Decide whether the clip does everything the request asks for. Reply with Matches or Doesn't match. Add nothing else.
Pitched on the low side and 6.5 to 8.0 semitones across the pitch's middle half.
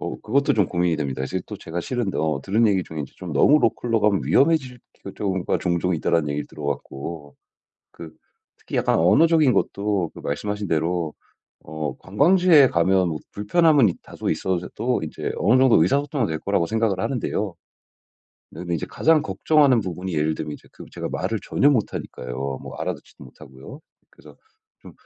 Matches